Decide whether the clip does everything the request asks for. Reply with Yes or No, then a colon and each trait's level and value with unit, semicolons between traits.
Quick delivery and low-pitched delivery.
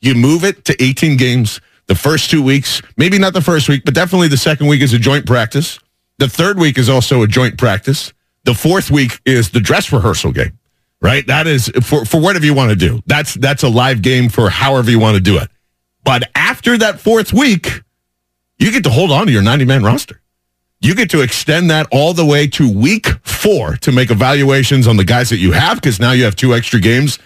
Yes: fast, 225 wpm; low, 130 Hz